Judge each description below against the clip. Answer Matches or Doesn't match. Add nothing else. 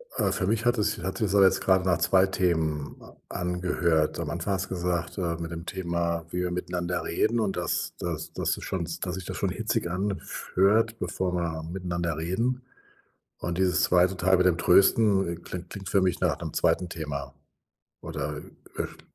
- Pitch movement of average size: Doesn't match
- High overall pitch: Doesn't match